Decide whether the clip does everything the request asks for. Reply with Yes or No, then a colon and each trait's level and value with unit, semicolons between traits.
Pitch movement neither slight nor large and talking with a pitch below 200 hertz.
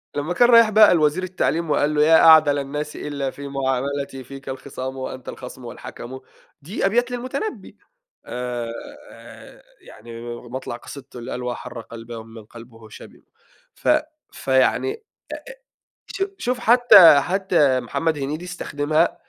No: wide, 6.0 semitones; medium, 140 Hz